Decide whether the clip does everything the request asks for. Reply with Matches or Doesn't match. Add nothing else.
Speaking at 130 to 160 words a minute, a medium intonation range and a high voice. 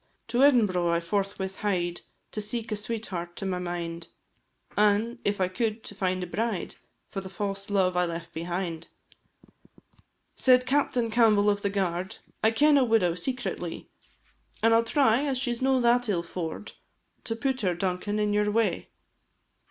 Doesn't match